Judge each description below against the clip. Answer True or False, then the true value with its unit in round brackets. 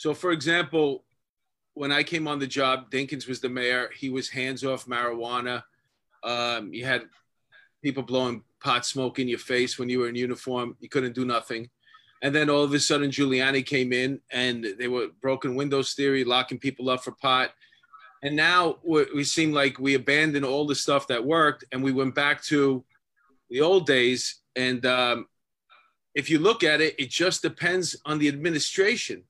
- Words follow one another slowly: False (185 wpm)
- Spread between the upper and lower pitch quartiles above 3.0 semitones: False (2.7 semitones)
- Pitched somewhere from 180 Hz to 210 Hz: False (135 Hz)